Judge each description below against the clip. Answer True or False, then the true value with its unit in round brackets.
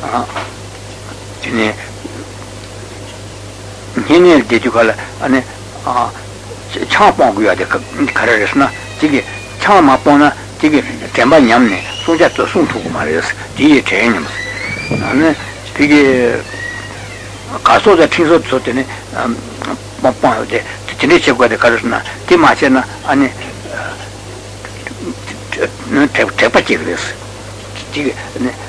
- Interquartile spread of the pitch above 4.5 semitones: False (4.0 semitones)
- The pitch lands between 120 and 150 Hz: False (105 Hz)